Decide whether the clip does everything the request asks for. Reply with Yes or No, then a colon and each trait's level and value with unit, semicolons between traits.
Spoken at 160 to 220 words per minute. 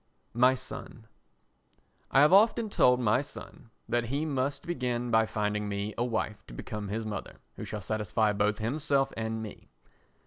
Yes: average, 165 wpm